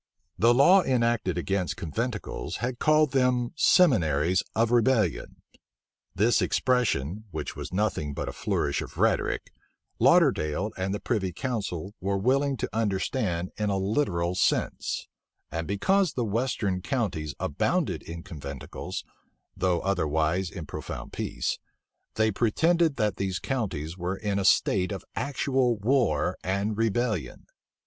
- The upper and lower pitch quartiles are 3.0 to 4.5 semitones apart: No, wide, 5.4 semitones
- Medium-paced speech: No, slow, 130 wpm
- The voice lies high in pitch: No, low, 100 Hz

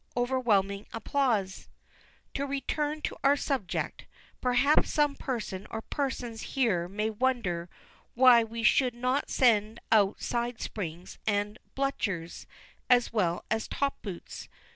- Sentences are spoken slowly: Yes, slow, 120 wpm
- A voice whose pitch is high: Yes, high, 235 Hz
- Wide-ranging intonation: No, average, 4.4 semitones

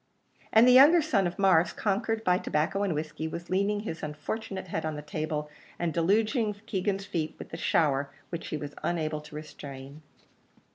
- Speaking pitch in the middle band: Yes, medium, 175 Hz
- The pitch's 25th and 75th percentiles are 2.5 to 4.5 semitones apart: No, average, 5.1 semitones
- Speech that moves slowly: No, average, 180 wpm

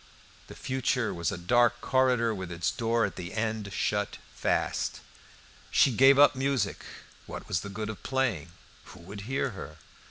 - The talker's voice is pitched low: Yes, low, 110 Hz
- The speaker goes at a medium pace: Yes, average, 165 wpm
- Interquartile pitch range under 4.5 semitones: No, average, 5.2 semitones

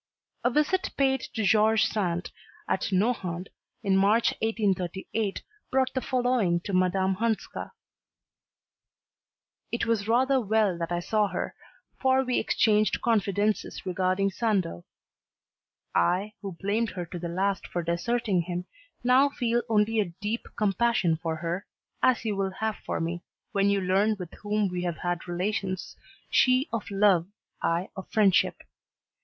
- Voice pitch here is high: Yes, high, 200 Hz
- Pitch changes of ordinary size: Yes, average, 3.9 semitones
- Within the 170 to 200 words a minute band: No, average, 145 wpm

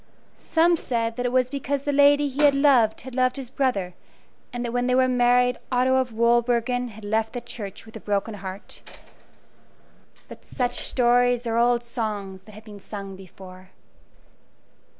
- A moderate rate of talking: Yes, average, 170 wpm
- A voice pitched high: Yes, high, 240 Hz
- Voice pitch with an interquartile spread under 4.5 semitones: Yes, average, 2.9 semitones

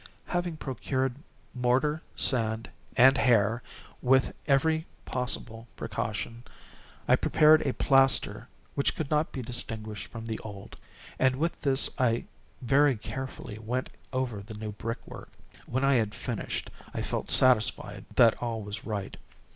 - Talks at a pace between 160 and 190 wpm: No, slow, 135 wpm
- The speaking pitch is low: Yes, low, 125 Hz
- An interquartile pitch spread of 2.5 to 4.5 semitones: Yes, average, 3.3 semitones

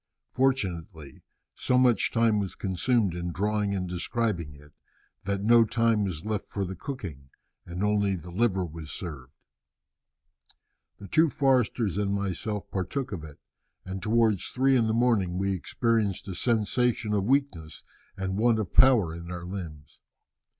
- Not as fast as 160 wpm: Yes, average, 150 wpm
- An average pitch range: Yes, average, 4.6 semitones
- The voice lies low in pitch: Yes, low, 100 Hz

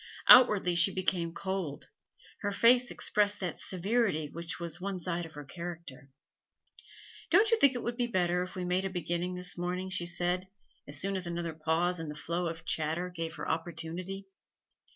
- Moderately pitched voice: Yes, medium, 180 Hz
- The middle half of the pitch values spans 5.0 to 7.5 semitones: No, narrow, 2.4 semitones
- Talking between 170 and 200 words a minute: Yes, average, 180 wpm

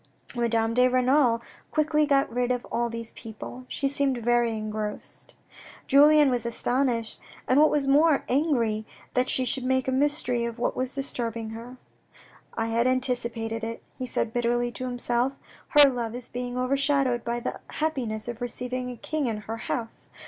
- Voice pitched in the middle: No, high, 245 Hz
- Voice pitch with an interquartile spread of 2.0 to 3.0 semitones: Yes, narrow, 2.5 semitones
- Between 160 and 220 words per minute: Yes, average, 175 wpm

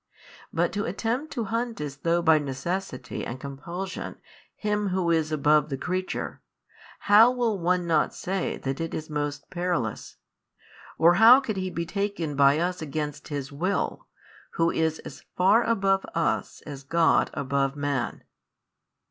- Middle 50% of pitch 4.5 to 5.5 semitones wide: Yes, average, 4.9 semitones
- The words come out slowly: No, average, 150 wpm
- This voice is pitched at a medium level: Yes, medium, 170 Hz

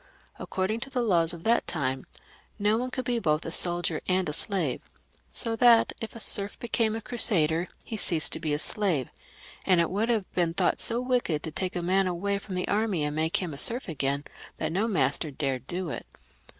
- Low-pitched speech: No, medium, 185 Hz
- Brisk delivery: Yes, fast, 215 wpm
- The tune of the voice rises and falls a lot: Yes, wide, 5.8 semitones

